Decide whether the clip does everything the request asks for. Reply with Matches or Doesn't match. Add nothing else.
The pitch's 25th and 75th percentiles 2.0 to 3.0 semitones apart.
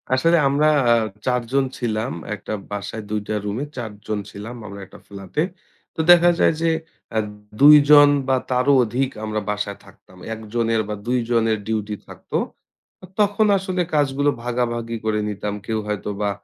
Doesn't match